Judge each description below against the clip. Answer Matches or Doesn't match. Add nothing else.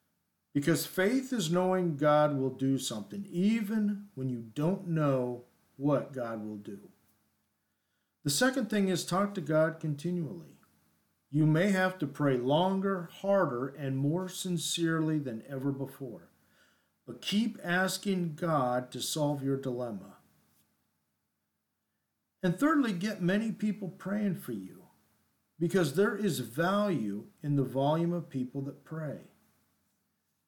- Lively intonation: Matches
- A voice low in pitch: Doesn't match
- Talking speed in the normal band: Doesn't match